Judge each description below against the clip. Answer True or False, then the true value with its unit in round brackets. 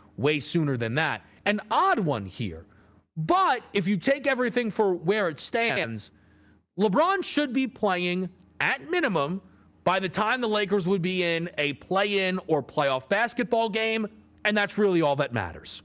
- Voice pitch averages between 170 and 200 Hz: True (185 Hz)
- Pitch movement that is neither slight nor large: False (7.2 semitones)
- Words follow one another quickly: False (165 wpm)